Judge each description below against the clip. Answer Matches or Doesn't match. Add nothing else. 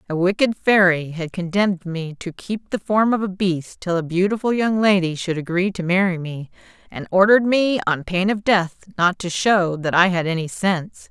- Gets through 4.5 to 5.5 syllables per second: Matches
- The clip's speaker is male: Doesn't match